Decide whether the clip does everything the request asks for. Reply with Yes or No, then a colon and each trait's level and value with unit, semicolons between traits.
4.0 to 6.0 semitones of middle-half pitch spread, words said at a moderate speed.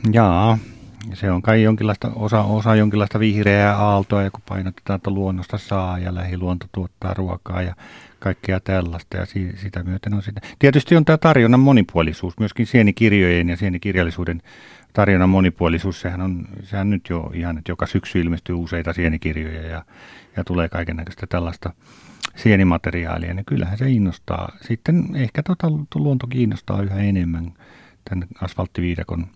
No: average, 3.4 semitones; average, 145 wpm